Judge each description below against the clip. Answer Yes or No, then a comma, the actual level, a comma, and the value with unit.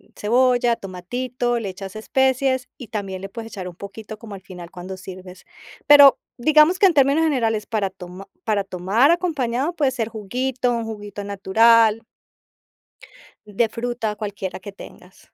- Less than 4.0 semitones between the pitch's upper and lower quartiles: No, average, 4.5 semitones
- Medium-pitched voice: No, high, 225 Hz